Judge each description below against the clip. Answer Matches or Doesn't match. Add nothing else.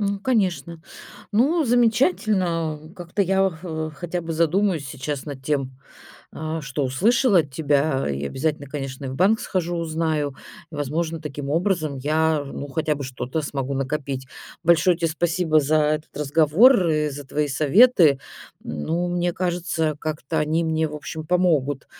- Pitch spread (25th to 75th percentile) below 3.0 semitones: Doesn't match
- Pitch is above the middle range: Doesn't match